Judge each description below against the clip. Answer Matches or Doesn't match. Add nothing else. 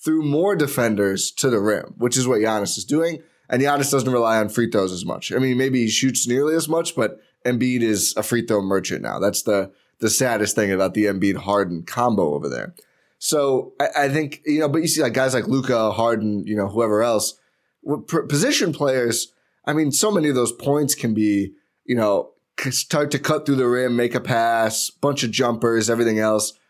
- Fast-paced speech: Matches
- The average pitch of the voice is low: Matches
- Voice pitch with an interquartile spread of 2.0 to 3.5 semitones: Doesn't match